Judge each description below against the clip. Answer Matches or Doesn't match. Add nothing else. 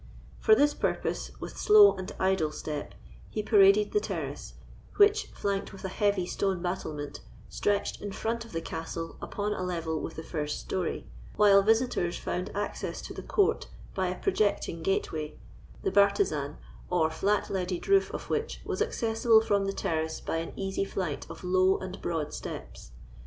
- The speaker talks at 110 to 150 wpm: Doesn't match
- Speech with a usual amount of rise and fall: Matches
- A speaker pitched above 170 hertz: Matches